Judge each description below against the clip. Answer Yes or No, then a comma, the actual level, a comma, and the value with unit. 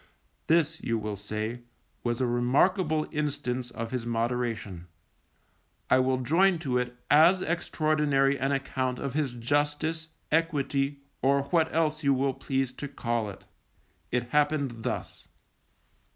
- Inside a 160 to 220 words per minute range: No, slow, 135 wpm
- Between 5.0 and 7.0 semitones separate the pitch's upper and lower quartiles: No, average, 3.8 semitones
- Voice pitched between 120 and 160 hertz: Yes, low, 135 Hz